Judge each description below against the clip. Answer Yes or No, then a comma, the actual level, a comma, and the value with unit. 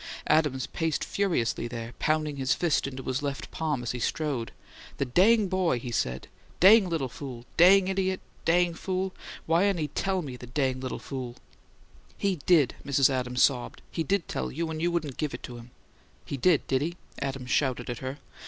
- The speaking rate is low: No, average, 190 wpm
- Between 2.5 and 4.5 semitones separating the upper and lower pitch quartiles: No, average, 5.3 semitones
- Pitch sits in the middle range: Yes, medium, 145 Hz